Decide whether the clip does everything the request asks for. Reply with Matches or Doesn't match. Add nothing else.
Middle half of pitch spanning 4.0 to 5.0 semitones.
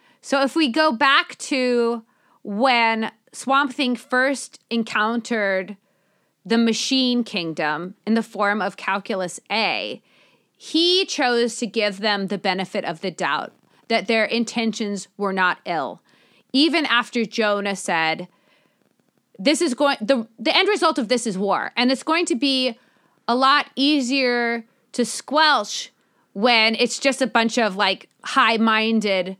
Matches